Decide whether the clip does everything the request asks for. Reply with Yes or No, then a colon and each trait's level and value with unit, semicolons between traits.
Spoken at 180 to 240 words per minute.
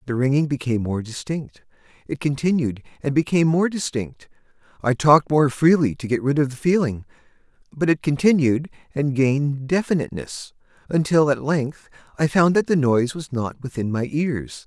No: average, 155 wpm